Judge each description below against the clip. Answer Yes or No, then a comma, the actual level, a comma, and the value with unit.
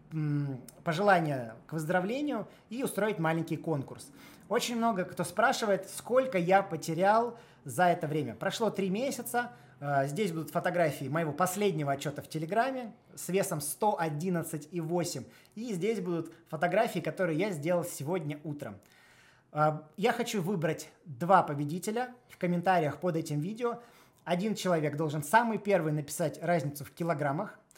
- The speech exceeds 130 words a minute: No, average, 125 wpm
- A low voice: No, medium, 175 Hz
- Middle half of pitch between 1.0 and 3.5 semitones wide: No, average, 4.8 semitones